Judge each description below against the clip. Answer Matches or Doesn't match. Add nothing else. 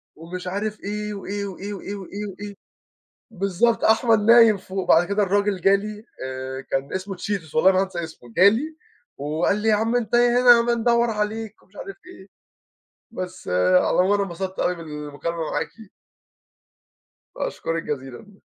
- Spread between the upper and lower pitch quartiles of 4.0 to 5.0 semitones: Doesn't match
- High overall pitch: Matches